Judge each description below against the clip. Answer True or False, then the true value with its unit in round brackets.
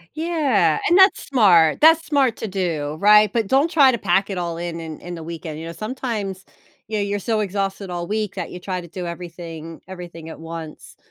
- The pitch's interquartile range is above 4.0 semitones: True (4.6 semitones)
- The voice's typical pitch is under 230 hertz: True (190 Hz)